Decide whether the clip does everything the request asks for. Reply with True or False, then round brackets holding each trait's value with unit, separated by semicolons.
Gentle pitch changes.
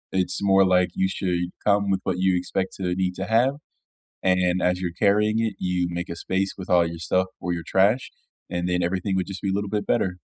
True (1.6 semitones)